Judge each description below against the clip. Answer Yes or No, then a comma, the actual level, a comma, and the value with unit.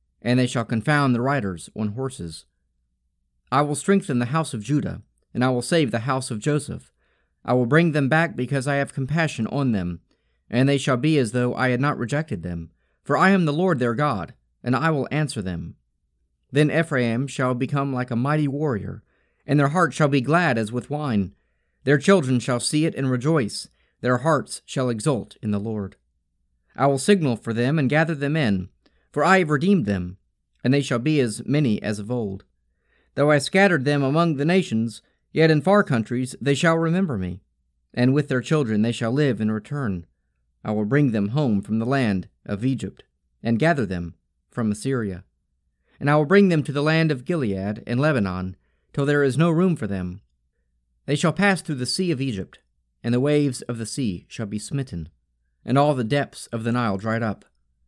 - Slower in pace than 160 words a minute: No, average, 200 wpm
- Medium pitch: No, low, 125 Hz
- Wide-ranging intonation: Yes, wide, 7.0 semitones